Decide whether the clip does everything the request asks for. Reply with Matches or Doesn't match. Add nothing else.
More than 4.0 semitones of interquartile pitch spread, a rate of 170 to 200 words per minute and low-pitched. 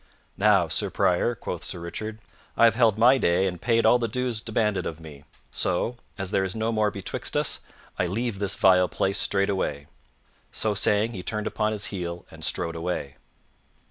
Doesn't match